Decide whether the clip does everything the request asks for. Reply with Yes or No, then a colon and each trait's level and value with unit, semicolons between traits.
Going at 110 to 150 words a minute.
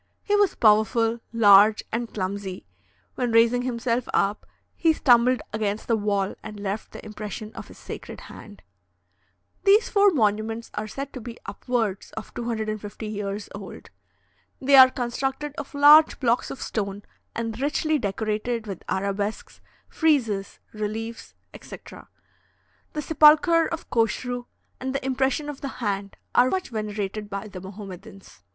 Yes: average, 140 wpm